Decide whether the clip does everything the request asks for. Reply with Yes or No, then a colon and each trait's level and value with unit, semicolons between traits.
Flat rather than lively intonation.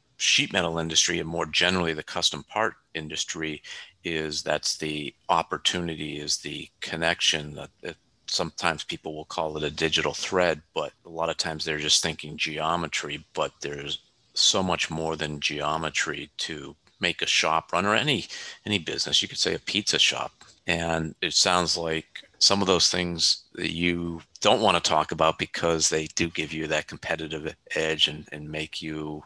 Yes: narrow, 1.4 semitones